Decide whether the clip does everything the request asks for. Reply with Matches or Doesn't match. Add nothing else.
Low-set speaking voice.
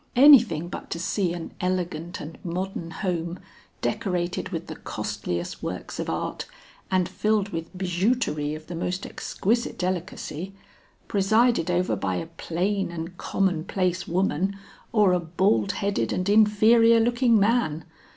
Doesn't match